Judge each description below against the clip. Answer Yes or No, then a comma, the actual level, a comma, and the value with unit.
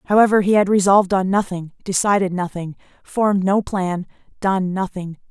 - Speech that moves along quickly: No, average, 145 wpm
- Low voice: No, high, 190 Hz